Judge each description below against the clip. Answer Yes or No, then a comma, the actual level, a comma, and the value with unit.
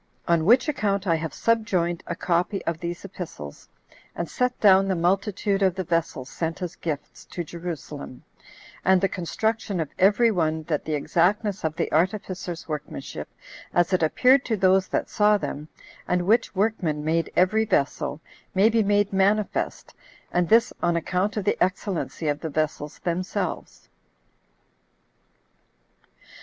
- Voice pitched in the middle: Yes, medium, 180 Hz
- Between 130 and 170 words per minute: Yes, average, 150 wpm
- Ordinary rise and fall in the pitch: Yes, average, 3.6 semitones